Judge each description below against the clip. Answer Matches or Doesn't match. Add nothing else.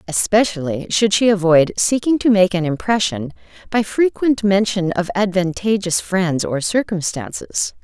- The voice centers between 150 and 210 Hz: Matches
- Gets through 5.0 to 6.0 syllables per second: Doesn't match